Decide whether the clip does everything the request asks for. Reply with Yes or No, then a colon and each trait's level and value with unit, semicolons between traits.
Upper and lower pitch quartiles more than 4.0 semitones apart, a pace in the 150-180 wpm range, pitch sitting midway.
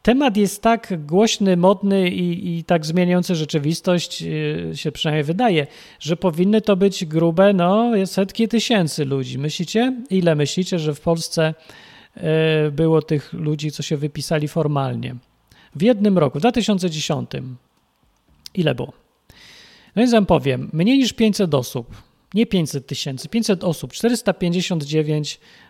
No: average, 4.6 semitones; average, 130 wpm; medium, 175 Hz